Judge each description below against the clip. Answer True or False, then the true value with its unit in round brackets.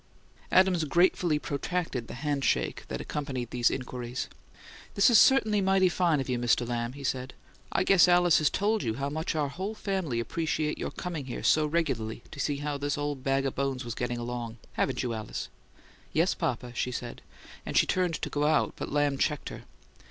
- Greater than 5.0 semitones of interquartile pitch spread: True (5.4 semitones)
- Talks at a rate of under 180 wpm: False (190 wpm)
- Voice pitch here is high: False (145 Hz)